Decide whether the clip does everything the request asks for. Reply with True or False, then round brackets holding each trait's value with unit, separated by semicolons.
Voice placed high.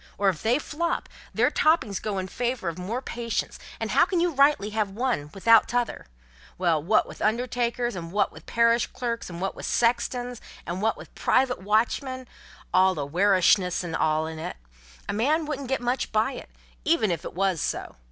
True (220 Hz)